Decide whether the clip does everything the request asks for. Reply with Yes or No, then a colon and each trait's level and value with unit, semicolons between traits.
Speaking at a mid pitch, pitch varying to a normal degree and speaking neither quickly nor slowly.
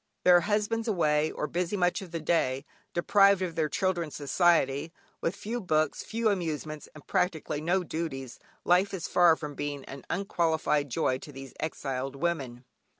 Yes: medium, 160 Hz; average, 3.8 semitones; average, 160 wpm